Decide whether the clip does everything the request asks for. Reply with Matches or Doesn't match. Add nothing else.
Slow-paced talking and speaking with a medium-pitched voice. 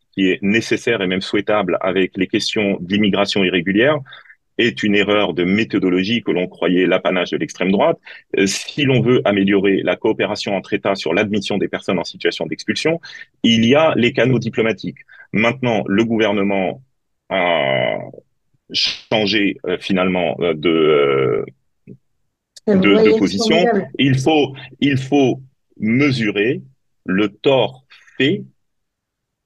Doesn't match